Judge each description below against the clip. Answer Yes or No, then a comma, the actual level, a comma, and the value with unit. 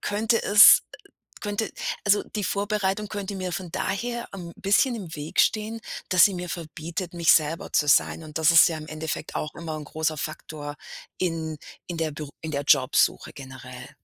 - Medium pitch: Yes, medium, 170 Hz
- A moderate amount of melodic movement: Yes, average, 4.7 semitones